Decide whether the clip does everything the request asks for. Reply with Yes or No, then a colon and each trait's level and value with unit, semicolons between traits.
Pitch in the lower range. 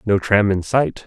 Yes: low, 100 Hz